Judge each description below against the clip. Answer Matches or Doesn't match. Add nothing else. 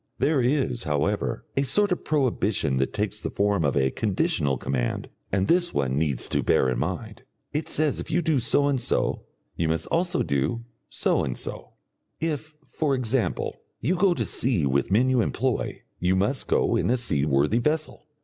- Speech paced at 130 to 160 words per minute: Doesn't match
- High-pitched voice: Doesn't match